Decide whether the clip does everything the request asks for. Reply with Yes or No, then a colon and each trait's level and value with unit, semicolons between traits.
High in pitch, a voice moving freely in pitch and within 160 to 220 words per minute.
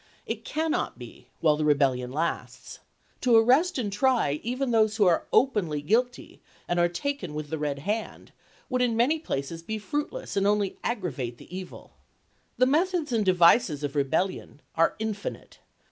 Yes: high, 200 Hz; wide, 8.4 semitones; average, 165 wpm